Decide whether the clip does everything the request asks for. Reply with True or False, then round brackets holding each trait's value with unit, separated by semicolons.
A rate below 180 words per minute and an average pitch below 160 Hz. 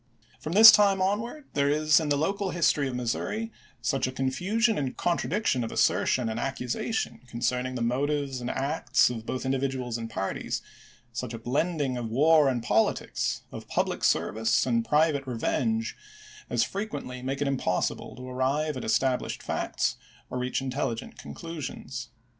True (160 wpm; 135 Hz)